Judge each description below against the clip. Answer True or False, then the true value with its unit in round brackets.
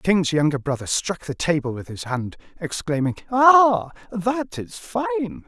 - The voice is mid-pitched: True (165 Hz)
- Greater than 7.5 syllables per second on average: False (4.5 syllables/s)